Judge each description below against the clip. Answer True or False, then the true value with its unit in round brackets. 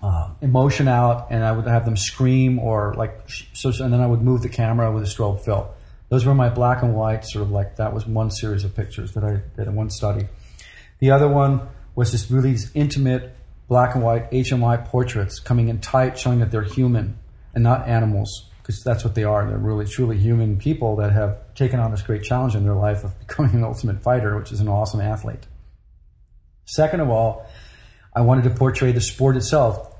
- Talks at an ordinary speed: False (215 wpm)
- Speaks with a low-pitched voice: True (115 Hz)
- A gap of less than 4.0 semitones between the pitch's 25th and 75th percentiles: True (3.1 semitones)